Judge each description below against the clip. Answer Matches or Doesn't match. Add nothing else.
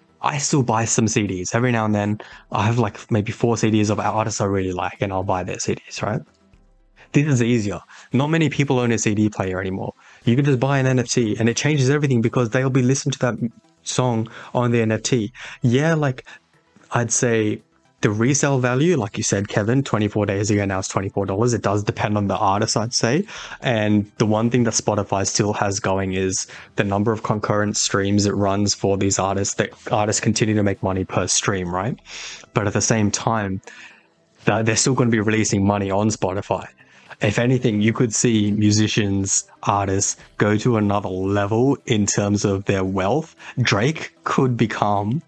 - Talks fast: Doesn't match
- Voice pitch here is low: Matches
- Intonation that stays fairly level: Doesn't match